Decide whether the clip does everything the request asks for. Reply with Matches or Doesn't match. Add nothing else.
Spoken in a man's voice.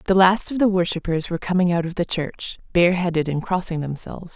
Doesn't match